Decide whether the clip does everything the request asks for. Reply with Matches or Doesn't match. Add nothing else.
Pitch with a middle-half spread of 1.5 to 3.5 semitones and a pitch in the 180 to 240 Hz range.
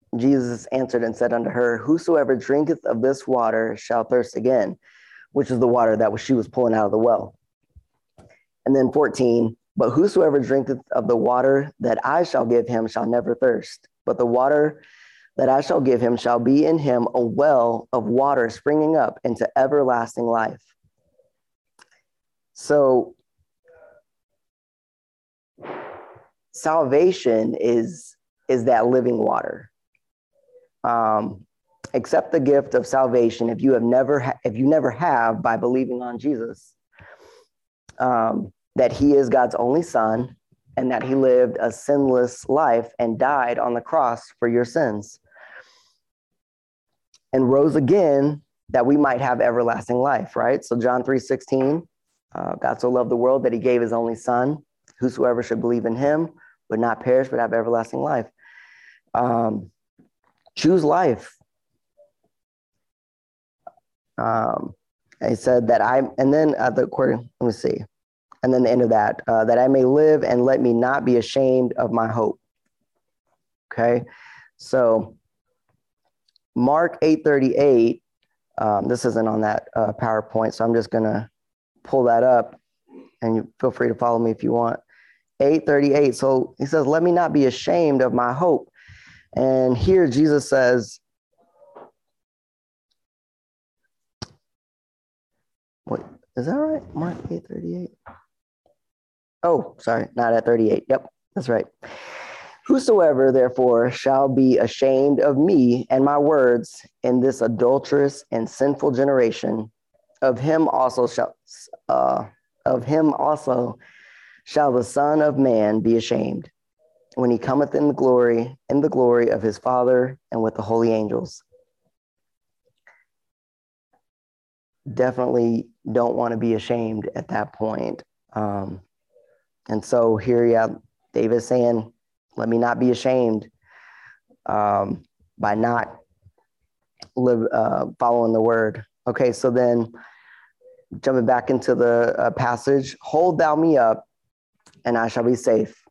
Doesn't match